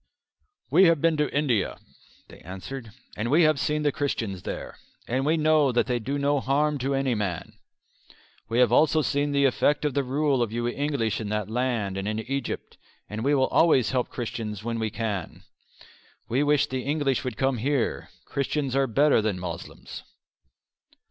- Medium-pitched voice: No, low, 130 Hz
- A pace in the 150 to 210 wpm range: Yes, average, 180 wpm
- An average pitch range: Yes, average, 4.3 semitones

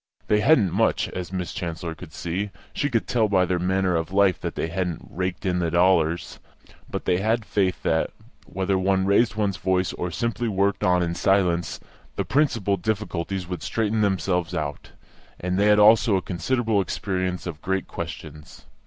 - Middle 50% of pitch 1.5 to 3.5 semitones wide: Yes, average, 2.8 semitones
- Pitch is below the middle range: Yes, very low, 95 Hz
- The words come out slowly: No, average, 180 wpm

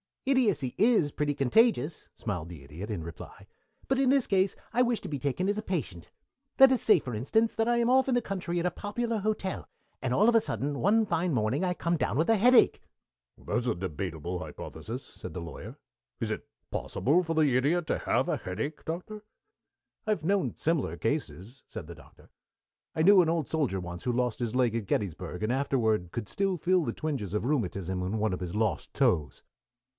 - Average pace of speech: No, fast, 210 wpm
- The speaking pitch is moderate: Yes, medium, 145 Hz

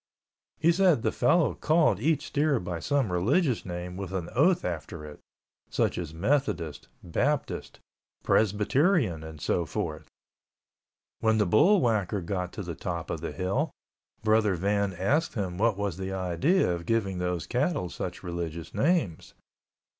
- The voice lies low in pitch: Yes, low, 100 Hz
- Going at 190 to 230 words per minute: No, average, 150 wpm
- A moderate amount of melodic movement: No, wide, 7.2 semitones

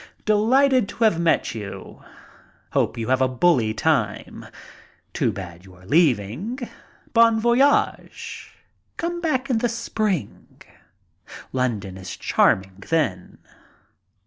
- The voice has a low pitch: No, medium, 160 Hz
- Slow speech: Yes, slow, 115 wpm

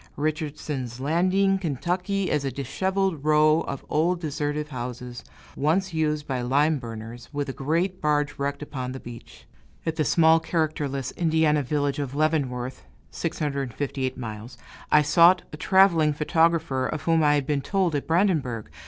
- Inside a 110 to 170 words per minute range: Yes, average, 150 wpm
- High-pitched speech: No, medium, 150 Hz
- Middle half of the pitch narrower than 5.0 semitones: Yes, average, 3.4 semitones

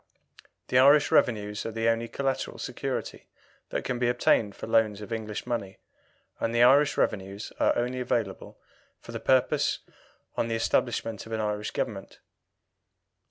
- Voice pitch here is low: Yes, low, 115 Hz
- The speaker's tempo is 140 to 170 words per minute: Yes, average, 150 wpm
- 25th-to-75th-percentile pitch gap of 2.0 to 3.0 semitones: Yes, narrow, 2.6 semitones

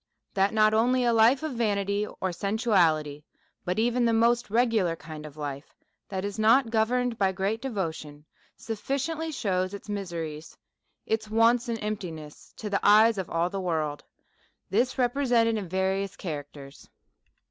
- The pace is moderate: Yes, average, 150 wpm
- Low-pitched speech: No, high, 205 Hz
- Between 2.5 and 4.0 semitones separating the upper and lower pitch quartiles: No, average, 4.6 semitones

